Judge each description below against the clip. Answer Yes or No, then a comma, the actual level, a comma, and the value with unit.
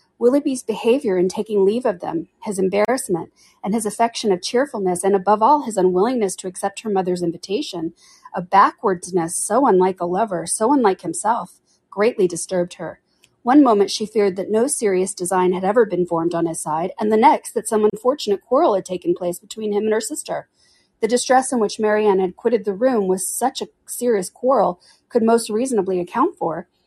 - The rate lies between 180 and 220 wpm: Yes, average, 190 wpm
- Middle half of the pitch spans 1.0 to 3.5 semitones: No, average, 4.0 semitones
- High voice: Yes, high, 205 Hz